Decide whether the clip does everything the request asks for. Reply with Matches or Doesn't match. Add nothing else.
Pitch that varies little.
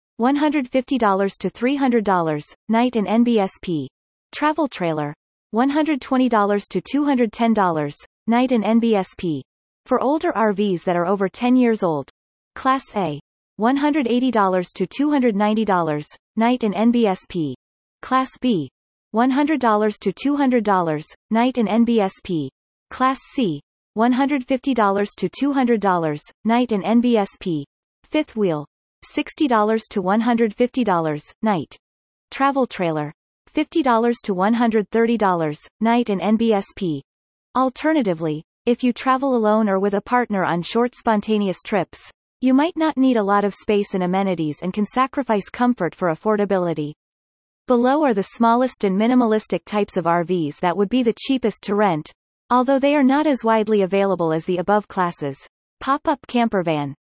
Doesn't match